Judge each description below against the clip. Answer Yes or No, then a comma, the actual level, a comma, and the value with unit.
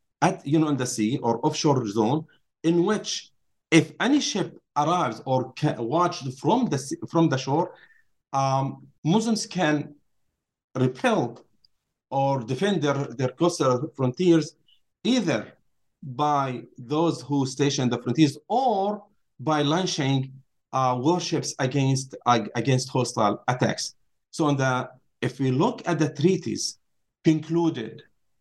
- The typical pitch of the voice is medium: Yes, medium, 145 Hz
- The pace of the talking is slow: Yes, slow, 125 wpm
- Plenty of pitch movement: No, average, 4.3 semitones